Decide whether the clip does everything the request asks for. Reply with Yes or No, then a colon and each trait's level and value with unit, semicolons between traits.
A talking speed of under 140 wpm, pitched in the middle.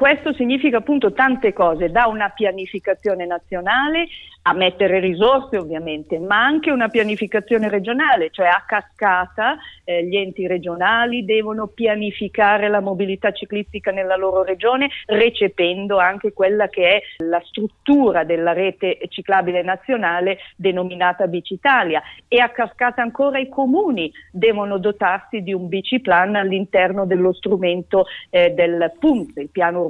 No: average, 130 wpm; high, 200 Hz